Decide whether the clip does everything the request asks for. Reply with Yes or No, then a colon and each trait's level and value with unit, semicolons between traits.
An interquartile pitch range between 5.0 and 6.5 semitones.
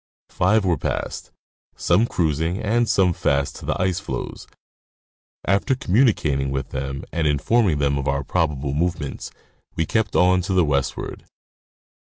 Yes: wide, 5.5 semitones